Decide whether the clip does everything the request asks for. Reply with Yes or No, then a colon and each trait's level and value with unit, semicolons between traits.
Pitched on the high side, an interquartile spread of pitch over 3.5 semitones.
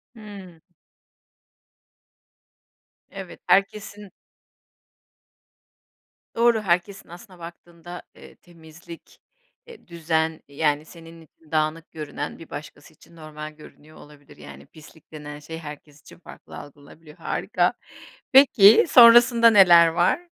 No: medium, 165 Hz; average, 4.1 semitones